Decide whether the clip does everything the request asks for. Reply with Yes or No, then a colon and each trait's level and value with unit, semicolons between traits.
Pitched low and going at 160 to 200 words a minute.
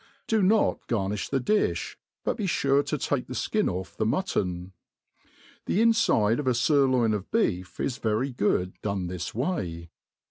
Yes: low, 120 Hz; average, 165 wpm